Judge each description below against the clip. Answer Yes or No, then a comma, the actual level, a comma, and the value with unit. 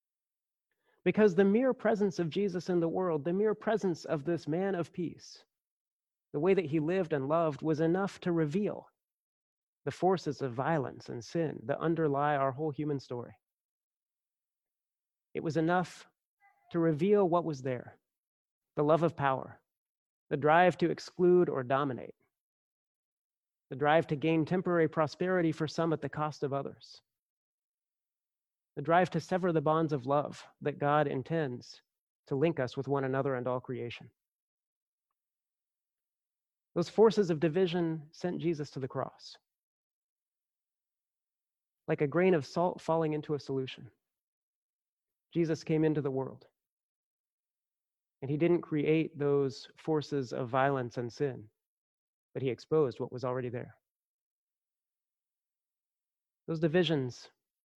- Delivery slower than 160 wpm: Yes, average, 140 wpm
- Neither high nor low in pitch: Yes, medium, 155 Hz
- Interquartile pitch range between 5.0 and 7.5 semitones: No, average, 3.9 semitones